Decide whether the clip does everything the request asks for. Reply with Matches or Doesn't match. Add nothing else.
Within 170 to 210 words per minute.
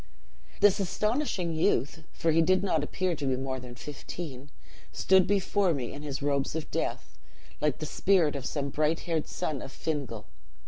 Matches